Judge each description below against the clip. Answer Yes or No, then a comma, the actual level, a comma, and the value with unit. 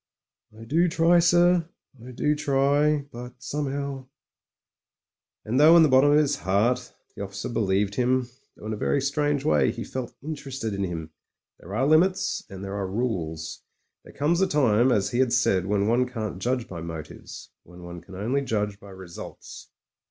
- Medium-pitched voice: No, low, 125 Hz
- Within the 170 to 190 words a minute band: Yes, average, 185 wpm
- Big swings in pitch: Yes, wide, 6.2 semitones